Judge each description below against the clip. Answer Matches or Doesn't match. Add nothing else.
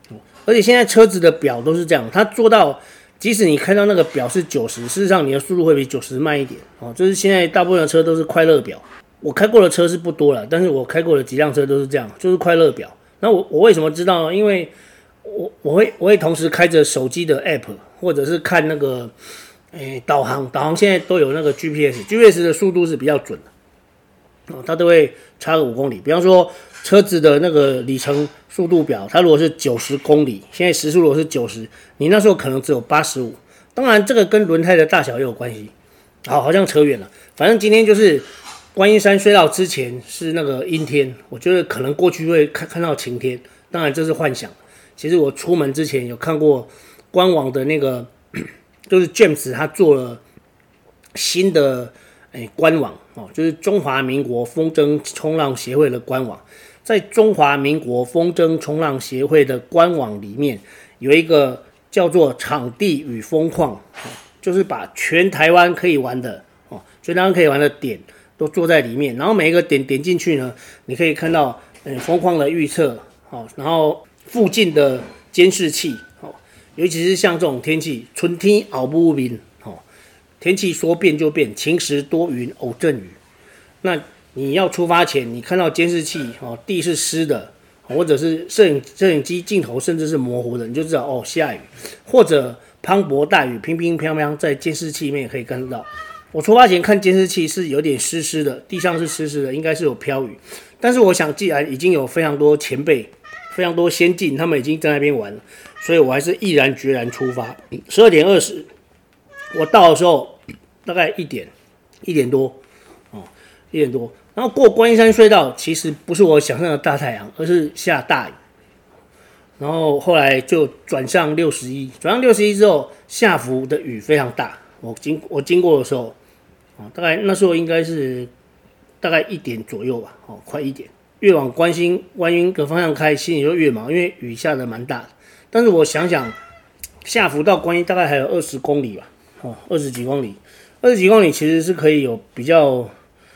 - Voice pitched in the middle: Matches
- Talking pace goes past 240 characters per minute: Matches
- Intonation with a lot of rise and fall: Doesn't match